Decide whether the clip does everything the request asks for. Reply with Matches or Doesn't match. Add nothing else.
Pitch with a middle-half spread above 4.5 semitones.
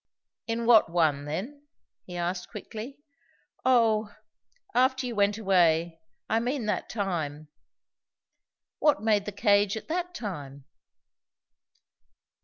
Matches